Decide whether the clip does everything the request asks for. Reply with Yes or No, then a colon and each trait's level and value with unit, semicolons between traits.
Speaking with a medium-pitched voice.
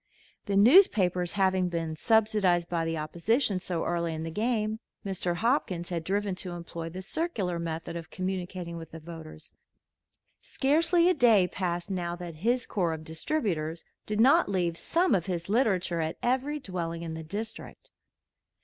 Yes: medium, 180 Hz